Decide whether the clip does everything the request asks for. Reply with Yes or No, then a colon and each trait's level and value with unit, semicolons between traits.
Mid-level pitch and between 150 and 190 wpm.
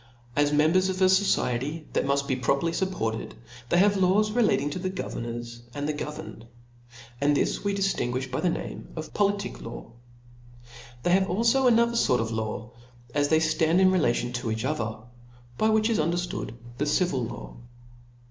Yes: medium, 155 Hz; average, 175 wpm